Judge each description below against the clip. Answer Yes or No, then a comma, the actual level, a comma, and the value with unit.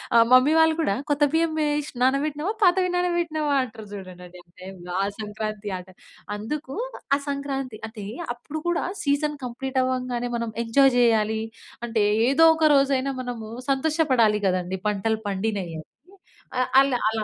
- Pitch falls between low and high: No, very high, 255 Hz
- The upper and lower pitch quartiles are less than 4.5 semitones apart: No, wide, 5.6 semitones